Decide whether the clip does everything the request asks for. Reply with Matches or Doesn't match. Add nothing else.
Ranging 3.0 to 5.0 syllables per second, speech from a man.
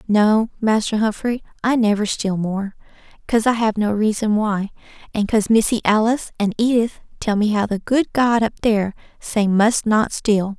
Doesn't match